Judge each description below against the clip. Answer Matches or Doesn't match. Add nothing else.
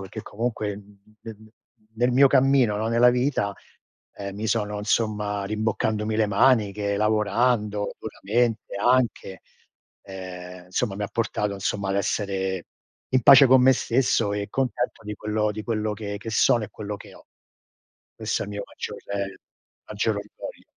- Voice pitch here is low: Matches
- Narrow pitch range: Matches